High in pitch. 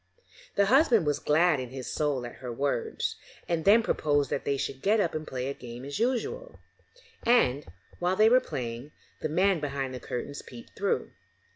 No: medium, 150 Hz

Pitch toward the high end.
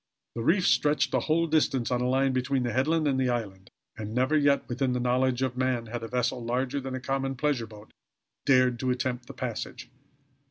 No: low, 130 Hz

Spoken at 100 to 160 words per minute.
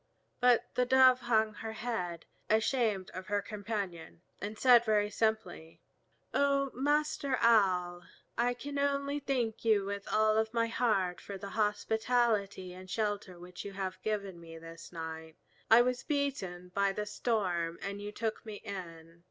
Yes: average, 150 wpm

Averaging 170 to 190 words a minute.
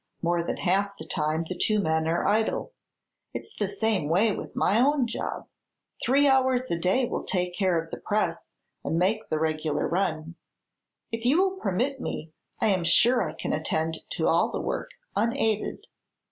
Yes: average, 180 wpm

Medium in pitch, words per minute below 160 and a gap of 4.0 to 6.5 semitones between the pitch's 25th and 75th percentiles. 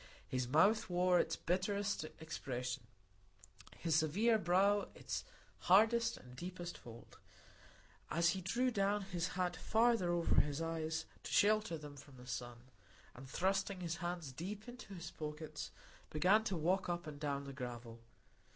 Yes: medium, 175 Hz; average, 150 wpm; average, 5.1 semitones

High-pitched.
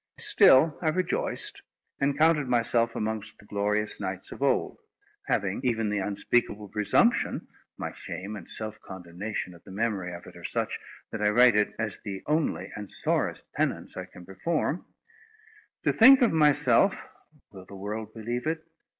No: low, 110 Hz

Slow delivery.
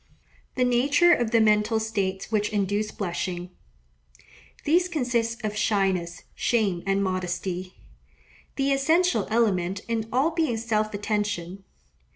Yes: slow, 115 wpm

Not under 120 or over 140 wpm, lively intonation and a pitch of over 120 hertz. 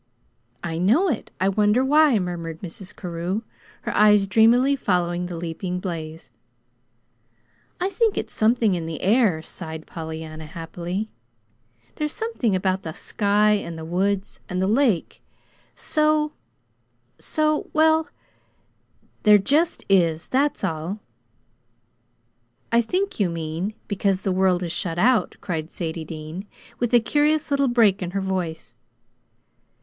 Yes: slow, 135 wpm; wide, 6.0 semitones; high, 190 Hz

